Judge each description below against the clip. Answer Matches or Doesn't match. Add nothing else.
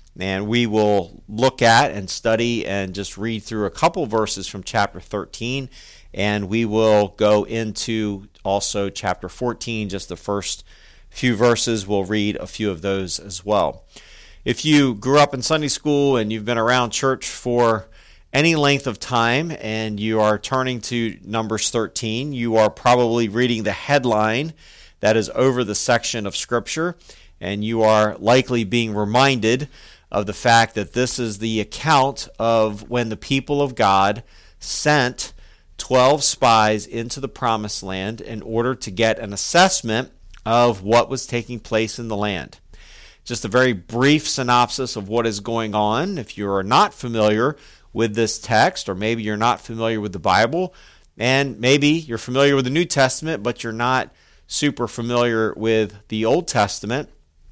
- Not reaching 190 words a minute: Matches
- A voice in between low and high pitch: Doesn't match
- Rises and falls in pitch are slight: Doesn't match